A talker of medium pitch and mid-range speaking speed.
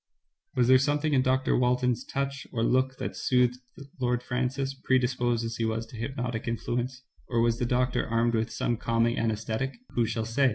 No: low, 125 Hz; average, 190 wpm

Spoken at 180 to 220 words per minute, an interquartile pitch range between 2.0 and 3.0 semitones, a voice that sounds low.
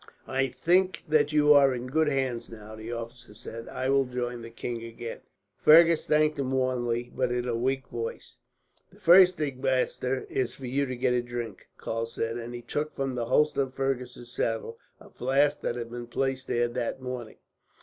Yes: average, 195 wpm; narrow, 2.4 semitones; low, 125 Hz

